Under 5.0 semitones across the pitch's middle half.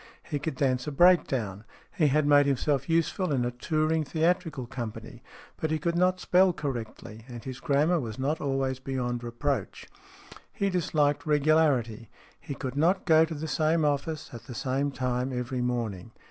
Yes: average, 4.3 semitones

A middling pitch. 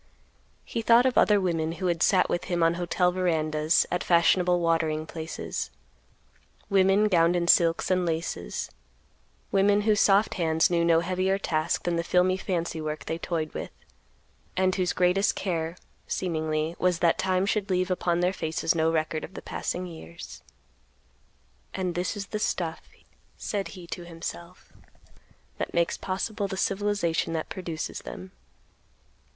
Yes: medium, 175 Hz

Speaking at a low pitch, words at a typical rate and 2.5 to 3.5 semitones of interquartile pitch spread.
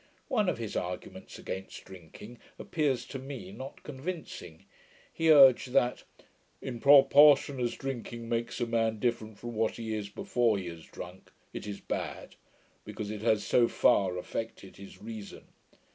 No: low, 115 Hz; average, 155 wpm; average, 4.4 semitones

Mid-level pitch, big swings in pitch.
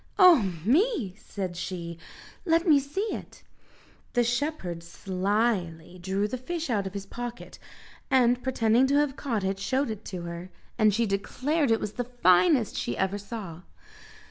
No: high, 220 Hz; wide, 5.7 semitones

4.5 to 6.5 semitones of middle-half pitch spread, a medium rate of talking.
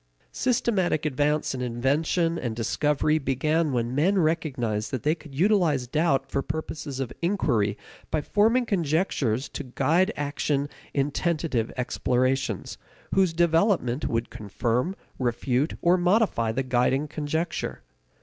No: average, 4.8 semitones; slow, 125 wpm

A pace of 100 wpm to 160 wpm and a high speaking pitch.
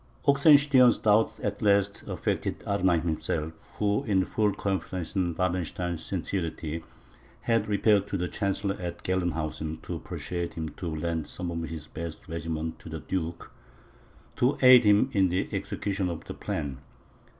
No: average, 150 wpm; very low, 90 Hz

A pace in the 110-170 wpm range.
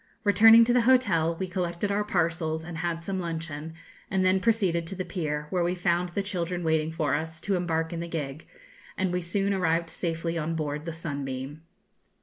No: average, 195 wpm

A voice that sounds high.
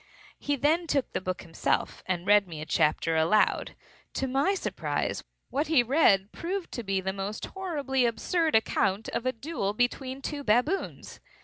Yes: high, 245 Hz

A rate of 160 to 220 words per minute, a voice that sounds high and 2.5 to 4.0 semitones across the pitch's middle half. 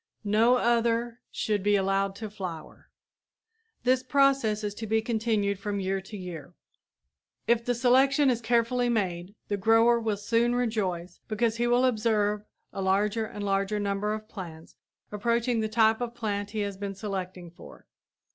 Yes: average, 165 wpm; high, 215 Hz; average, 2.9 semitones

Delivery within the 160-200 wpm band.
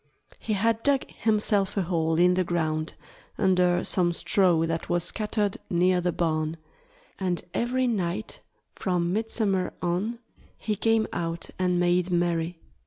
No: average, 140 wpm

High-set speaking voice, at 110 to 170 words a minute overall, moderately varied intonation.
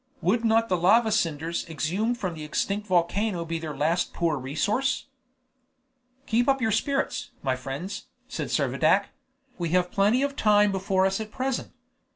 Yes: high, 195 Hz; average, 160 wpm; average, 5.0 semitones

